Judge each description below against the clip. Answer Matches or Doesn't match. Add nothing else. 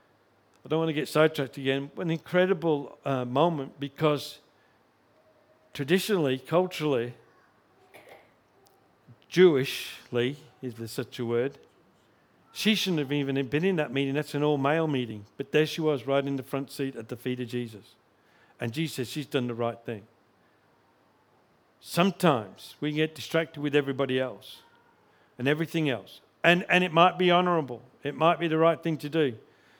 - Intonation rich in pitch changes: Doesn't match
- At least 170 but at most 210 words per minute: Doesn't match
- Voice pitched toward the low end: Doesn't match